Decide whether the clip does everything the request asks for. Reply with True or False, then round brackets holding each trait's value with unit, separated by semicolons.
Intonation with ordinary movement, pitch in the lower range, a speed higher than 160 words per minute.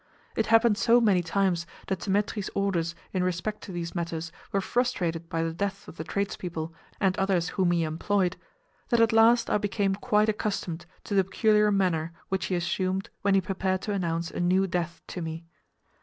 False (3.1 semitones; 190 Hz; 185 wpm)